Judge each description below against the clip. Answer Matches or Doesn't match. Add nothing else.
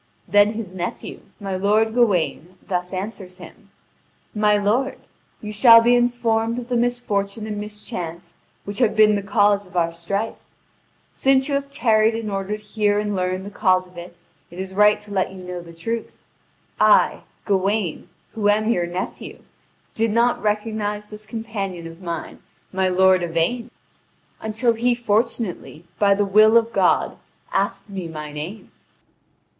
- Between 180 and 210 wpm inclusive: Doesn't match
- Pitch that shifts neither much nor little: Matches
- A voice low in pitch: Doesn't match